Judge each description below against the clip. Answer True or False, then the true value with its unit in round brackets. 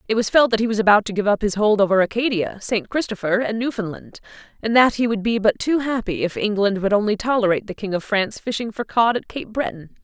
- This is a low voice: False (215 Hz)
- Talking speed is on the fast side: True (245 wpm)